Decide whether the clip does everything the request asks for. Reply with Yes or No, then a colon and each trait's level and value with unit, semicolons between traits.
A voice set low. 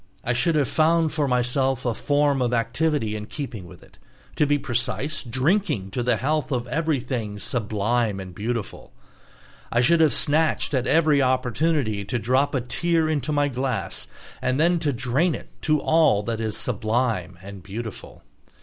Yes: low, 130 Hz